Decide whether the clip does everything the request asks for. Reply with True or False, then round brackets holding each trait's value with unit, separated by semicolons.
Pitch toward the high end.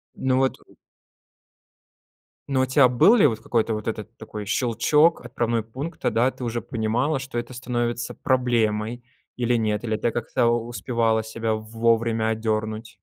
False (115 Hz)